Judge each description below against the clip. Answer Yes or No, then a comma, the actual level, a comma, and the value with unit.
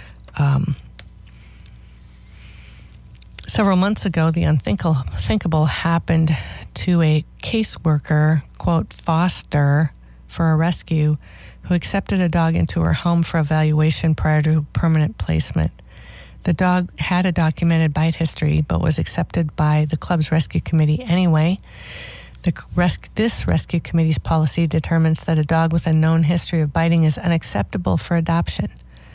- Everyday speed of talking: No, slow, 130 wpm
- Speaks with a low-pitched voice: No, medium, 160 Hz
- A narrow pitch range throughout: Yes, narrow, 1.8 semitones